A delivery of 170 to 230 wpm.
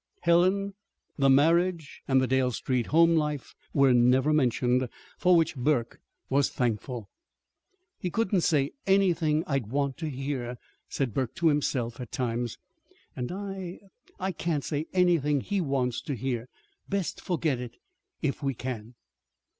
No: average, 145 wpm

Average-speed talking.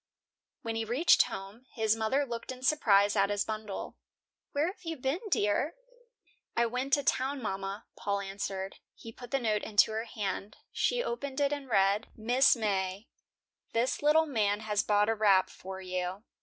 Yes: average, 170 wpm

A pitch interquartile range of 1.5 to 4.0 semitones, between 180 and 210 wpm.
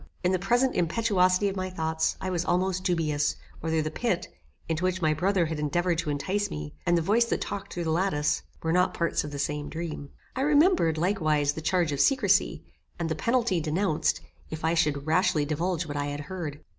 Yes: average, 3.5 semitones; fast, 205 wpm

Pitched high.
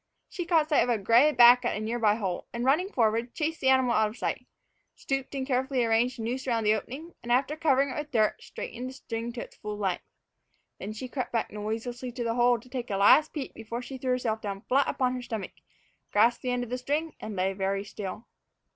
Yes: high, 245 Hz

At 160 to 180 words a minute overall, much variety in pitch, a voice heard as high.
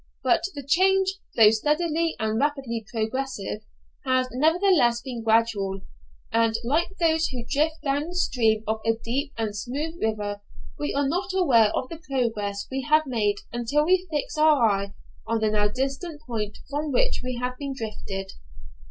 Yes: average, 165 wpm; wide, 5.7 semitones; very high, 255 Hz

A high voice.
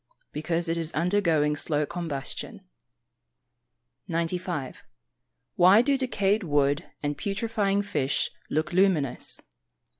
No: medium, 170 Hz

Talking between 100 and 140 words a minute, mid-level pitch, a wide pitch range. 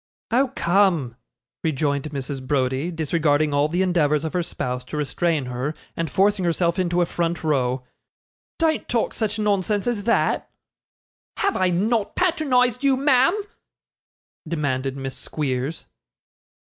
Yes: slow, 135 wpm; medium, 170 Hz; wide, 6.5 semitones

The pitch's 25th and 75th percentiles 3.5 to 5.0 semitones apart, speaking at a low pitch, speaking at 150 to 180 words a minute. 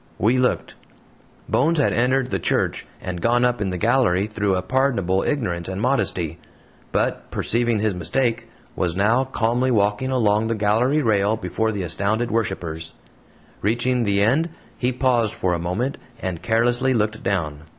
Yes: average, 4.6 semitones; low, 110 Hz; average, 160 wpm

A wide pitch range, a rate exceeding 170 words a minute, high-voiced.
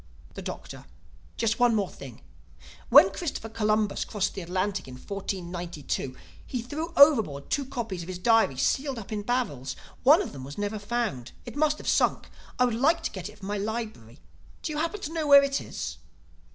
Yes: wide, 6.6 semitones; average, 190 wpm; high, 220 Hz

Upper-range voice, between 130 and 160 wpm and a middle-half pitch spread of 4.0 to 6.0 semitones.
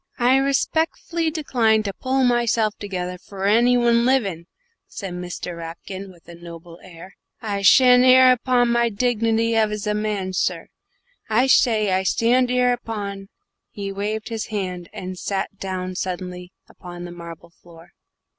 Yes: high, 210 Hz; average, 155 wpm; average, 4.7 semitones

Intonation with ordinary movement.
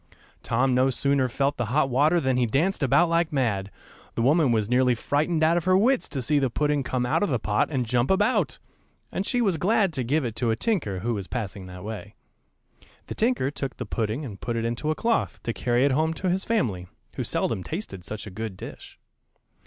No: wide, 5.7 semitones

